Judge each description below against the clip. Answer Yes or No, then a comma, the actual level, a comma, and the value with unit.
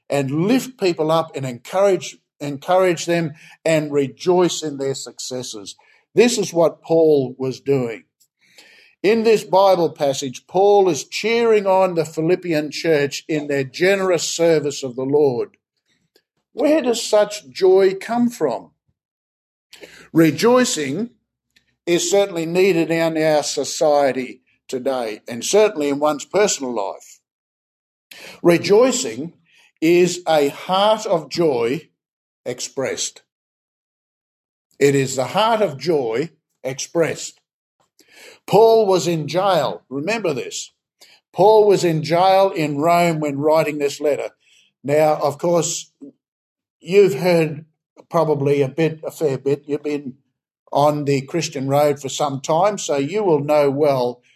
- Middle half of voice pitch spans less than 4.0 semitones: No, average, 5.0 semitones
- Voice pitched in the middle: Yes, medium, 160 Hz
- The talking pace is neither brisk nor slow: No, slow, 125 wpm